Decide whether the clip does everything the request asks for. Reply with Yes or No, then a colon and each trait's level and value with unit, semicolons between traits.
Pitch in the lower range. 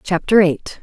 No: medium, 180 Hz